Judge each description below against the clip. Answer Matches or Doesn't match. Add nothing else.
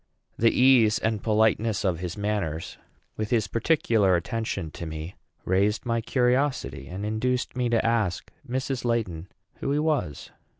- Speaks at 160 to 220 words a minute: Doesn't match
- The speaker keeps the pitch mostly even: Doesn't match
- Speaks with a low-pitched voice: Matches